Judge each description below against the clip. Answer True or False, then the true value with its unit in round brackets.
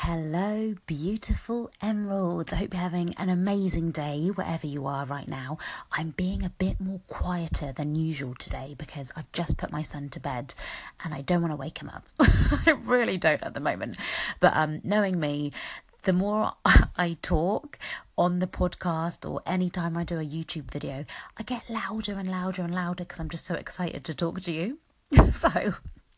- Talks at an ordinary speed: True (190 wpm)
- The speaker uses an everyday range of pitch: True (3.5 semitones)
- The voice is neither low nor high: True (175 Hz)